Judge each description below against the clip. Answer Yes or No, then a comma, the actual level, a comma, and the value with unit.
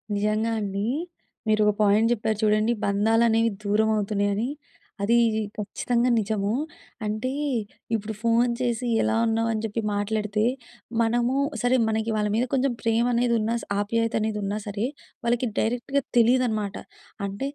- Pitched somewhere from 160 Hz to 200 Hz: No, high, 220 Hz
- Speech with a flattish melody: Yes, narrow, 2.0 semitones